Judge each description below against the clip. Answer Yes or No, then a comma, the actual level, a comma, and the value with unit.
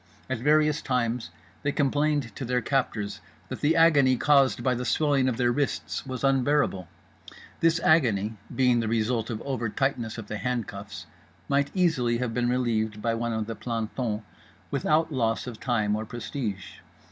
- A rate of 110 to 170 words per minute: Yes, average, 160 wpm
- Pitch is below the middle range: Yes, low, 125 Hz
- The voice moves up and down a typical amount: Yes, average, 3.7 semitones